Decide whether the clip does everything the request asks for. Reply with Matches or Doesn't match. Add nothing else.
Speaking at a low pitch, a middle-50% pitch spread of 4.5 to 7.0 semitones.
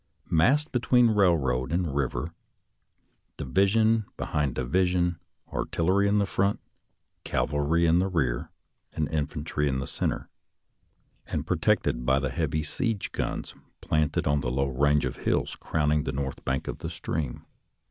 Matches